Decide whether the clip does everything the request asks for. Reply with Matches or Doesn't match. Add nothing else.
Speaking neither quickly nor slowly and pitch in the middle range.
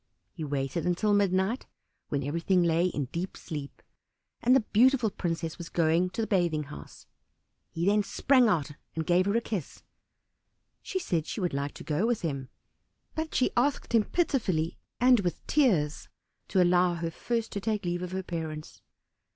Matches